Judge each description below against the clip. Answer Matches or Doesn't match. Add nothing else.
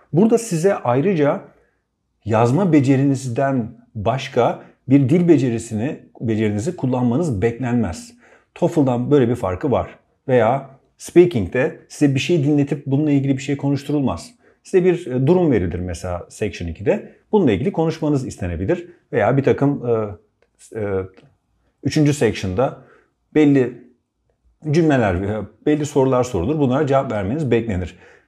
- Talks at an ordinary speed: Matches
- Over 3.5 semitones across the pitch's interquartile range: Matches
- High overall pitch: Doesn't match